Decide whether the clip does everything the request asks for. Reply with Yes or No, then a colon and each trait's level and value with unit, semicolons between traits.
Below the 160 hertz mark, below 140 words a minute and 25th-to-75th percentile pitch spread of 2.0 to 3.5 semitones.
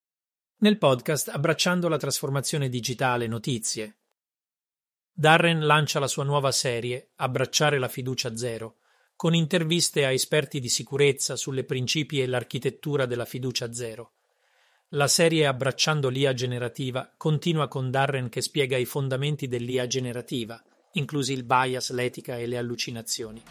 Yes: low, 135 Hz; average, 130 wpm; average, 3.1 semitones